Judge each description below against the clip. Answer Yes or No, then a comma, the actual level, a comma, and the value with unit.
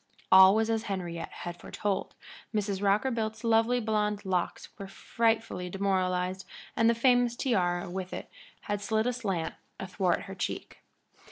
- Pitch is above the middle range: Yes, high, 200 Hz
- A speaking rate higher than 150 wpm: No, average, 140 wpm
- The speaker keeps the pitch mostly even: No, average, 3.2 semitones